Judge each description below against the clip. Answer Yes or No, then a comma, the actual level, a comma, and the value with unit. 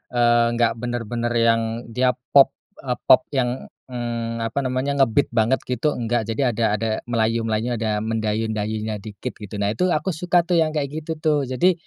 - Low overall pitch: Yes, low, 120 Hz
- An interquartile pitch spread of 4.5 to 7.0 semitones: No, average, 2.9 semitones